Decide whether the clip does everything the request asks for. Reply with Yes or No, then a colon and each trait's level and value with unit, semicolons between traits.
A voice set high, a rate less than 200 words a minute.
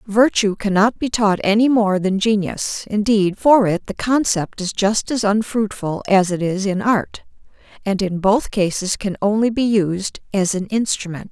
Yes: high, 205 Hz; average, 175 wpm